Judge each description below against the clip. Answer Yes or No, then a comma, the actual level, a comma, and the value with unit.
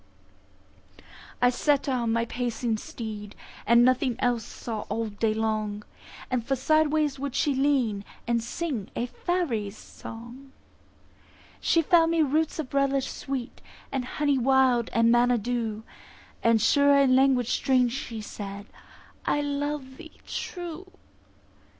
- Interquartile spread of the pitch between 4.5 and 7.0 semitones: No, average, 3.7 semitones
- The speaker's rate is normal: No, slow, 130 wpm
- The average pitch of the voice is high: Yes, very high, 250 Hz